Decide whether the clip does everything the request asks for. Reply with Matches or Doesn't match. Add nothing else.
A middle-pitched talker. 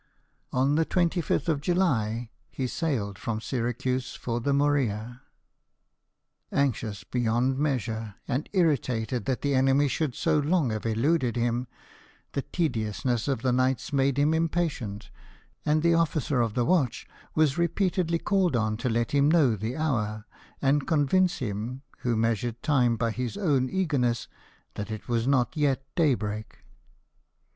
Doesn't match